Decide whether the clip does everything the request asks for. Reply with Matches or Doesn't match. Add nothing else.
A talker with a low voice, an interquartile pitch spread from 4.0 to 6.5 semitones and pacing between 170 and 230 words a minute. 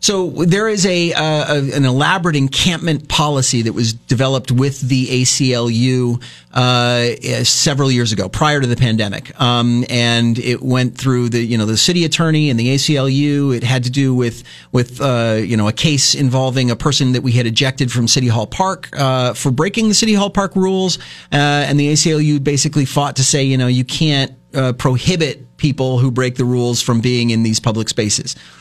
Doesn't match